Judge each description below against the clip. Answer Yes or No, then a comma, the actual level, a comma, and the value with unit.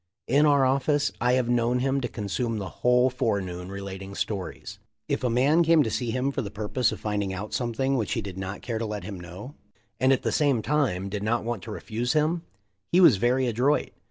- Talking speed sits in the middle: No, fast, 225 wpm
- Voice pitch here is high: No, low, 120 Hz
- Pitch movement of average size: Yes, average, 4.5 semitones